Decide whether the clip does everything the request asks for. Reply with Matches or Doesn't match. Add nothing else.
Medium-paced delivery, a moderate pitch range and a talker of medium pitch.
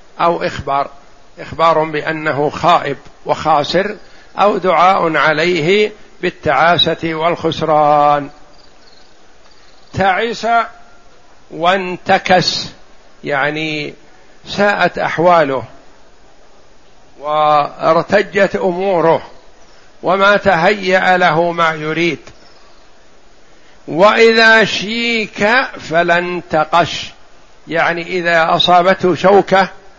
Doesn't match